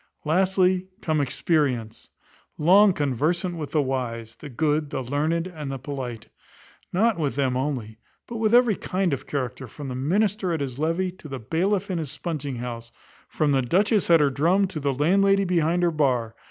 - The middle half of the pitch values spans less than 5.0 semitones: No, wide, 5.4 semitones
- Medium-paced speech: Yes, average, 180 wpm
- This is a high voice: No, medium, 150 Hz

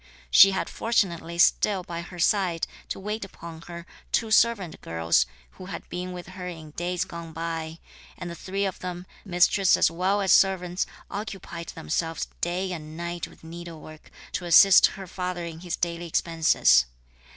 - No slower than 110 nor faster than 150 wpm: No, average, 165 wpm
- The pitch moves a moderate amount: No, narrow, 2.2 semitones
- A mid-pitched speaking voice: Yes, medium, 175 Hz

